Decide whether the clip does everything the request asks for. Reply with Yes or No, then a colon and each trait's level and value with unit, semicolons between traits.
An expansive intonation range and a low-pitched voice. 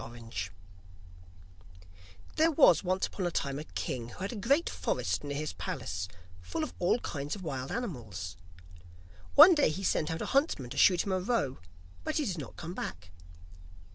No: wide, 8.7 semitones; medium, 160 Hz